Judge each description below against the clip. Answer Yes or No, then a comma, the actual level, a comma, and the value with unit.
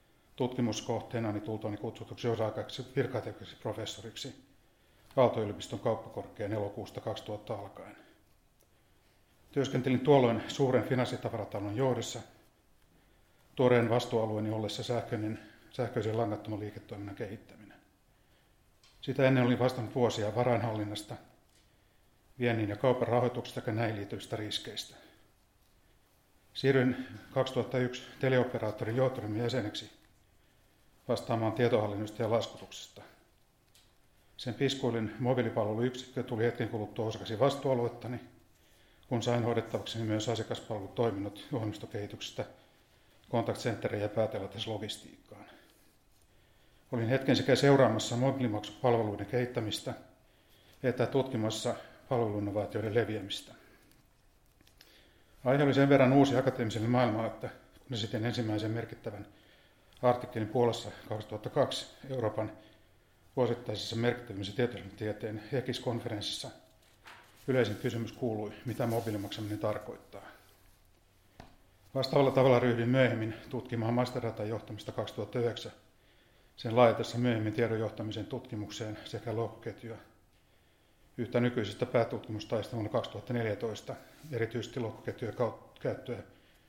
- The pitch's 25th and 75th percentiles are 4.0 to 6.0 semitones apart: No, average, 2.7 semitones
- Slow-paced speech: Yes, slow, 90 wpm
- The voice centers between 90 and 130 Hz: Yes, low, 115 Hz